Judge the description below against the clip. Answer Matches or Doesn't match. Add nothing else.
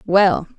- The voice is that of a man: Doesn't match